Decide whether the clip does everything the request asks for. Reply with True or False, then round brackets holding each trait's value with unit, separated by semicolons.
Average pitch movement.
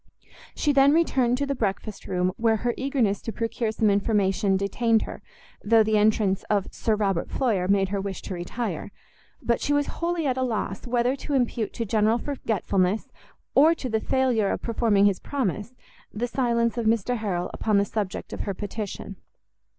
True (3.6 semitones)